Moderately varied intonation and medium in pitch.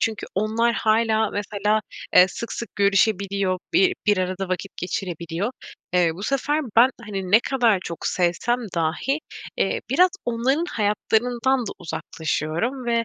No: average, 4.4 semitones; high, 210 Hz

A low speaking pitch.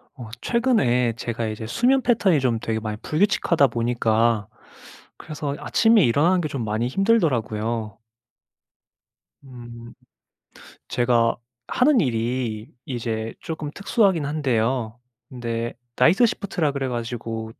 Yes: low, 125 Hz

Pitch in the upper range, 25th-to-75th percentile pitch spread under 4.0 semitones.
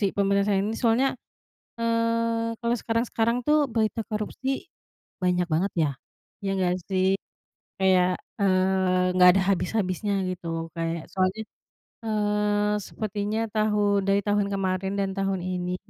Yes: high, 200 Hz; average, 2.9 semitones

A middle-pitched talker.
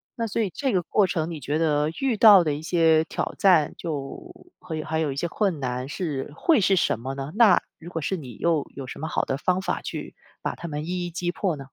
Yes: medium, 165 Hz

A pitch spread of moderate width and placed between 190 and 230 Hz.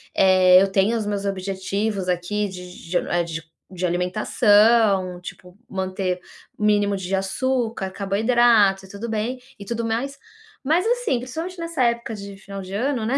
Yes: average, 3.8 semitones; high, 200 Hz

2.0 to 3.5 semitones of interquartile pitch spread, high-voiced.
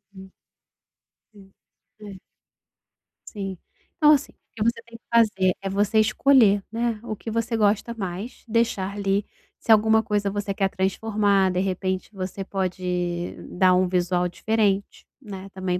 Yes: average, 2.8 semitones; high, 200 Hz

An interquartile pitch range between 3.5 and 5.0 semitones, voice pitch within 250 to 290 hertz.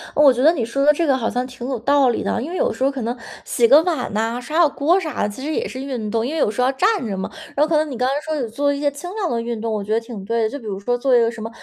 Yes: average, 4.1 semitones; very high, 255 Hz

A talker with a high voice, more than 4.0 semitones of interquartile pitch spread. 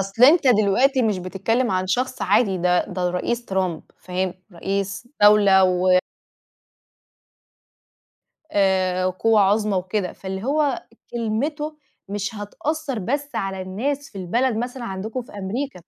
Yes: high, 205 Hz; average, 4.6 semitones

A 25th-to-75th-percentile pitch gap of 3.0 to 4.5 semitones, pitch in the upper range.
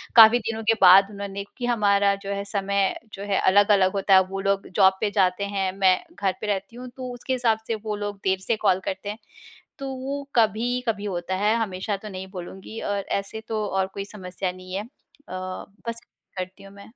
No: narrow, 2.4 semitones; high, 200 Hz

